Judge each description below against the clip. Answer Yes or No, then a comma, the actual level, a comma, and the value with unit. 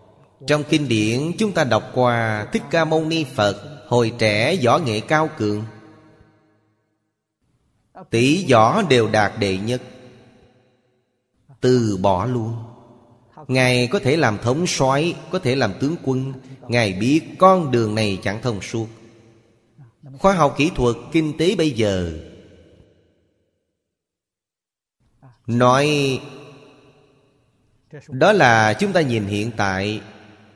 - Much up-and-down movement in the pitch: No, average, 4.7 semitones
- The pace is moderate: No, slow, 120 wpm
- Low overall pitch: Yes, low, 125 Hz